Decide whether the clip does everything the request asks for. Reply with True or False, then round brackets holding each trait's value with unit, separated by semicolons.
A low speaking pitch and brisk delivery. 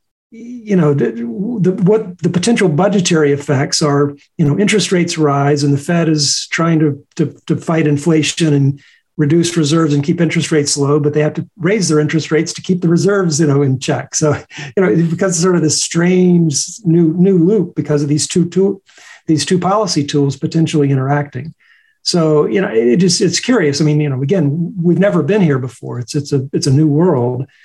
False (160 Hz; 210 wpm)